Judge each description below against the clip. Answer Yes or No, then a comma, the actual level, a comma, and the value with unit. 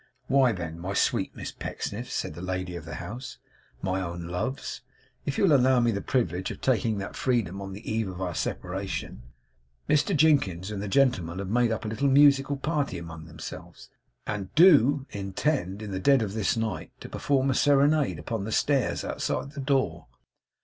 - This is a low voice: Yes, low, 110 Hz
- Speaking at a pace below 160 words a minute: No, average, 190 wpm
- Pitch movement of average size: No, wide, 6.7 semitones